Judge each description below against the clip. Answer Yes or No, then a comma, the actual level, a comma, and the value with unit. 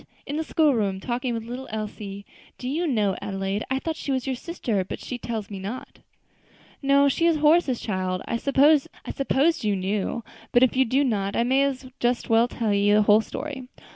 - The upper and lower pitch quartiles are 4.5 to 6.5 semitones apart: Yes, average, 5.0 semitones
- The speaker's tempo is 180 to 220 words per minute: Yes, average, 200 wpm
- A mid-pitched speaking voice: No, high, 240 Hz